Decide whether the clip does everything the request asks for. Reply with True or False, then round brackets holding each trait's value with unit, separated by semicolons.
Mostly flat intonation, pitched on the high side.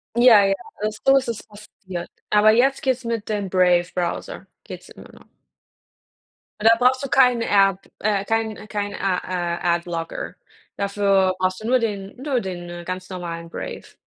False (3.7 semitones; 200 Hz)